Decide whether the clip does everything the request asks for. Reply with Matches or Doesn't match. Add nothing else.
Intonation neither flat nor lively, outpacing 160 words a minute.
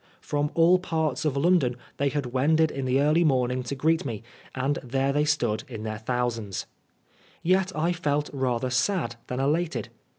Matches